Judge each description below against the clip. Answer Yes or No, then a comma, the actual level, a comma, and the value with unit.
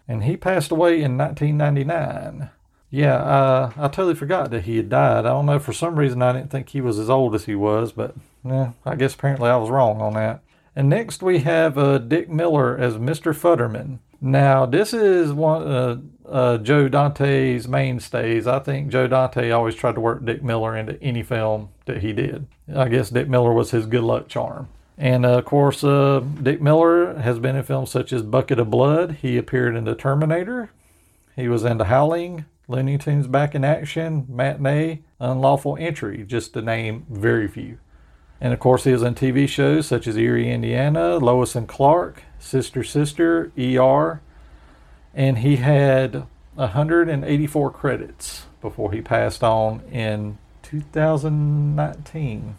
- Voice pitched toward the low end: Yes, low, 130 Hz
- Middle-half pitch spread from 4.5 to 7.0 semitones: No, average, 3.8 semitones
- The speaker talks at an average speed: Yes, average, 175 wpm